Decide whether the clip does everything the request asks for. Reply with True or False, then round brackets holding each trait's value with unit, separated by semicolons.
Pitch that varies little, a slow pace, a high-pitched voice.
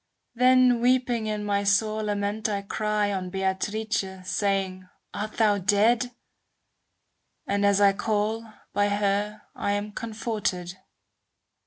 True (1.6 semitones; 120 wpm; 205 Hz)